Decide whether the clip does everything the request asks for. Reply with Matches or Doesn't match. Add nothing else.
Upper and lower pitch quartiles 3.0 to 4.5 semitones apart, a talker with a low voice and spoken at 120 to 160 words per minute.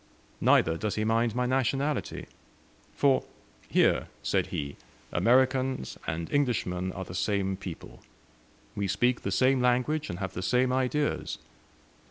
Doesn't match